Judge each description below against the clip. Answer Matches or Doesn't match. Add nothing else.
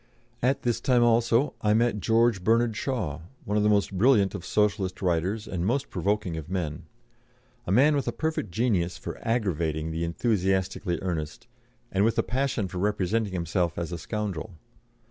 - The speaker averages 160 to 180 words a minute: Matches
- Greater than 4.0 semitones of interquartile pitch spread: Matches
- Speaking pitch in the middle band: Doesn't match